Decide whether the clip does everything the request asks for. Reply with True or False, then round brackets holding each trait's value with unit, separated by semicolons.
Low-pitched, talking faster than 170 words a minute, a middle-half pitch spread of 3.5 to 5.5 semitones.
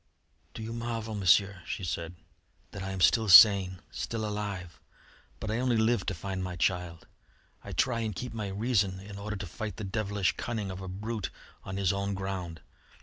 False (100 Hz; 190 wpm; 2.7 semitones)